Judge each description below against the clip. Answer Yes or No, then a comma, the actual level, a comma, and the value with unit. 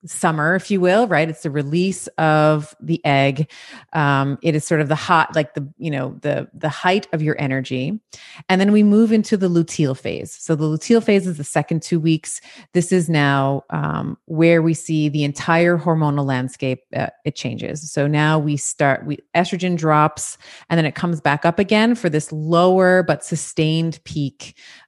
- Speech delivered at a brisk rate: No, average, 190 wpm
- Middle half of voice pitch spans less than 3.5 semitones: Yes, average, 2.9 semitones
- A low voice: No, medium, 155 Hz